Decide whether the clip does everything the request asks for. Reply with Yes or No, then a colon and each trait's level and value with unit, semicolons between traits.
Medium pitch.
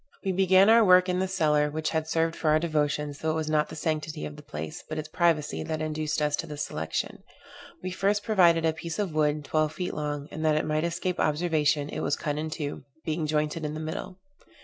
Yes: medium, 155 Hz